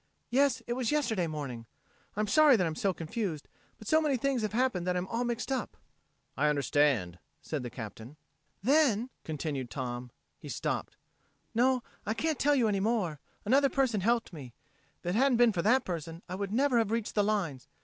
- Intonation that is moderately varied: No, wide, 7.9 semitones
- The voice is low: No, high, 210 Hz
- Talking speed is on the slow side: No, average, 190 wpm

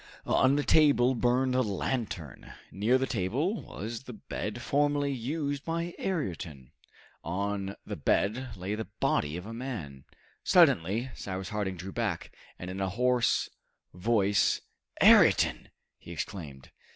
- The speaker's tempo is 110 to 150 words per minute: Yes, slow, 135 wpm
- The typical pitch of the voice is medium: No, low, 110 Hz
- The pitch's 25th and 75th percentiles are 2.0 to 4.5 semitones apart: No, wide, 5.6 semitones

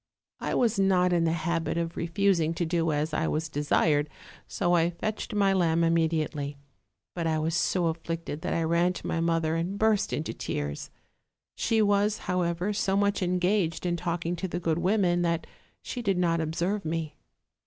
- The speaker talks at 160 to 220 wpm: Yes, average, 185 wpm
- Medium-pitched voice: Yes, medium, 170 Hz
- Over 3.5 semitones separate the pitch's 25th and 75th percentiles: No, narrow, 2.6 semitones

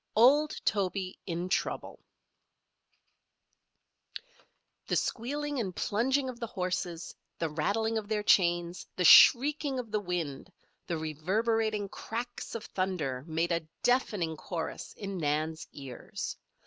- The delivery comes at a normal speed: No, slow, 120 wpm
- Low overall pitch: No, high, 190 Hz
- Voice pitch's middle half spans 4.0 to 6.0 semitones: Yes, wide, 5.4 semitones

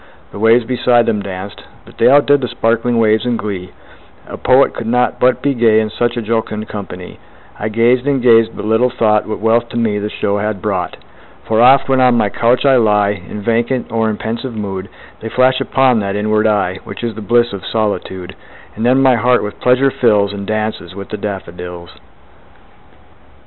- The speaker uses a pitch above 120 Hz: No, low, 110 Hz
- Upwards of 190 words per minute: Yes, average, 200 wpm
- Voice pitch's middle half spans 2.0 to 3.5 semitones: Yes, average, 2.9 semitones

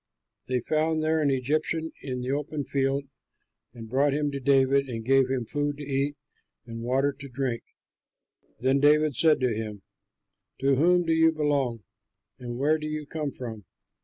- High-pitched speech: No, medium, 140 Hz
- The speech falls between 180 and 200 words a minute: No, average, 170 wpm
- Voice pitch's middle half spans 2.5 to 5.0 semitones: Yes, average, 3.0 semitones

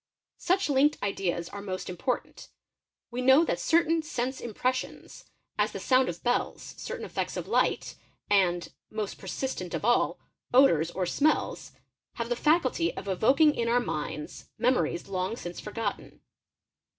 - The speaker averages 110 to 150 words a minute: Yes, average, 140 wpm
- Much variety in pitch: Yes, wide, 6.1 semitones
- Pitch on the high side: Yes, high, 235 Hz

